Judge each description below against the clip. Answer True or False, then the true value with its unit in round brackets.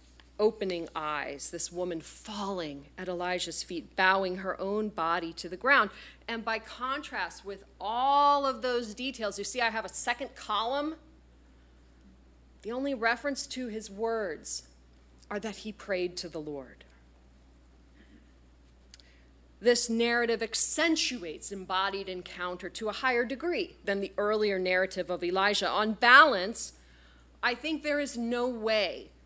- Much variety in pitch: True (7.9 semitones)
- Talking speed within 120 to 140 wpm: True (135 wpm)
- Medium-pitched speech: False (195 Hz)